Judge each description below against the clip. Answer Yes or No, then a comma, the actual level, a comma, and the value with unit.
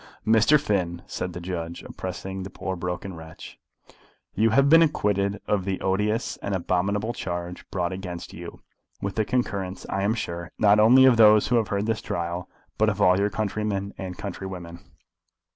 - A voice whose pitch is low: Yes, low, 100 Hz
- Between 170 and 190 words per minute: Yes, average, 175 wpm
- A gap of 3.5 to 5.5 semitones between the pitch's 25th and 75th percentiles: No, average, 3.0 semitones